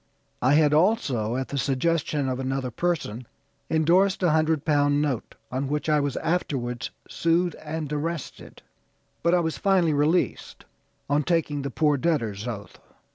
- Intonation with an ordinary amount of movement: Yes, average, 3.8 semitones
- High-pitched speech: No, medium, 150 Hz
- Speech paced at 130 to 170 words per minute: Yes, average, 150 wpm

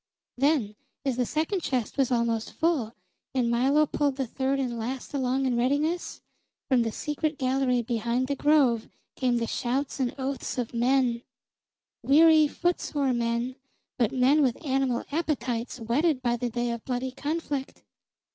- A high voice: Yes, very high, 260 Hz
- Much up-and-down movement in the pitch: No, average, 3.1 semitones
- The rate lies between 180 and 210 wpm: No, average, 155 wpm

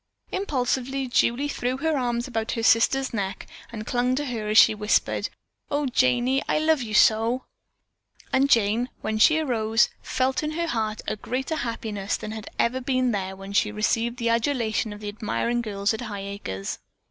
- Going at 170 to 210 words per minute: Yes, average, 180 wpm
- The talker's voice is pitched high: Yes, high, 235 Hz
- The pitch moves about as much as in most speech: Yes, average, 3.4 semitones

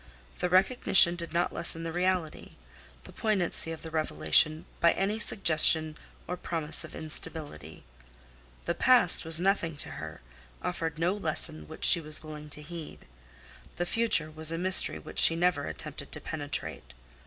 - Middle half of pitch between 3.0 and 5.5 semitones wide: No, narrow, 2.4 semitones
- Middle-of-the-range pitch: Yes, medium, 165 Hz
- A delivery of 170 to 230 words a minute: No, average, 155 wpm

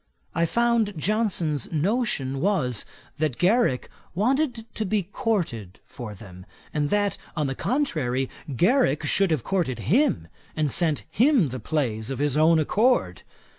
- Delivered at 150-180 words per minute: No, average, 140 wpm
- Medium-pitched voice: Yes, medium, 160 Hz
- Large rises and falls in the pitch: Yes, wide, 8.3 semitones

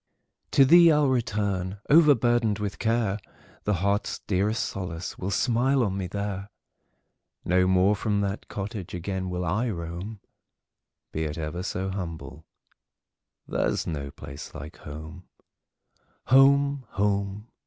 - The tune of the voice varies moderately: Yes, average, 3.8 semitones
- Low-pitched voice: Yes, low, 100 Hz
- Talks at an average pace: No, slow, 120 wpm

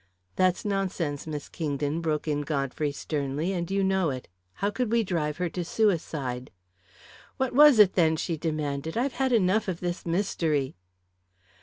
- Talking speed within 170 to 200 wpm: No, average, 160 wpm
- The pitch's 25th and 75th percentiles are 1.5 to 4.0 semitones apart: No, average, 4.7 semitones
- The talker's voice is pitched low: No, medium, 170 Hz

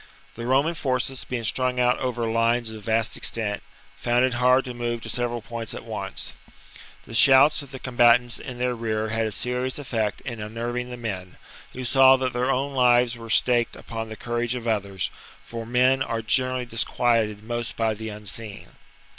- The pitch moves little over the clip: Yes, narrow, 2.0 semitones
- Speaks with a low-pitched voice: Yes, low, 120 Hz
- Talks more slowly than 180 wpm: No, average, 190 wpm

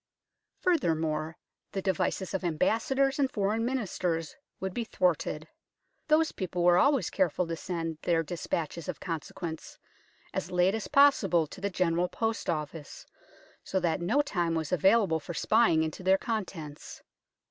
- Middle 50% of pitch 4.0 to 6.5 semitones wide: Yes, average, 4.8 semitones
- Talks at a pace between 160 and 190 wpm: No, average, 145 wpm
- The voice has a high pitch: No, medium, 180 Hz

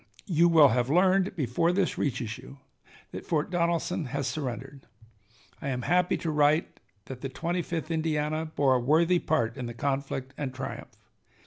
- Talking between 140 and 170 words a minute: Yes, average, 165 wpm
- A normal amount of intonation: Yes, average, 4.2 semitones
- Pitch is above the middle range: No, medium, 150 Hz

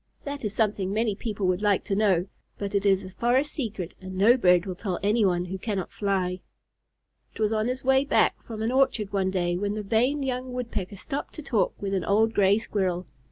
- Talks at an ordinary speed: No, fast, 215 wpm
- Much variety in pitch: No, average, 3.7 semitones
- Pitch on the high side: Yes, high, 205 Hz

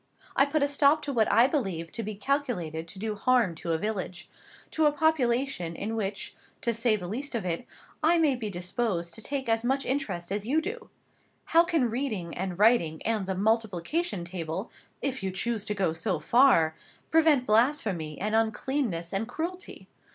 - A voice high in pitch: Yes, high, 225 Hz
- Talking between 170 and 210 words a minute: Yes, average, 190 wpm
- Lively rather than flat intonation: Yes, wide, 6.9 semitones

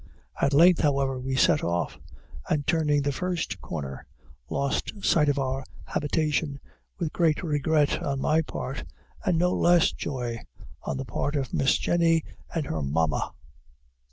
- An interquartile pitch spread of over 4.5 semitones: No, average, 3.4 semitones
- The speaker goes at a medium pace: Yes, average, 150 wpm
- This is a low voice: No, medium, 145 Hz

